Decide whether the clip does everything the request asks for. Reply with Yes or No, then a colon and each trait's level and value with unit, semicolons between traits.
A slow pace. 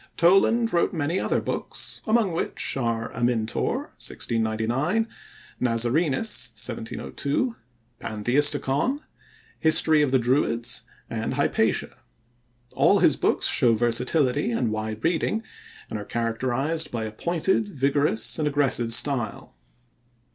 Yes: slow, 110 wpm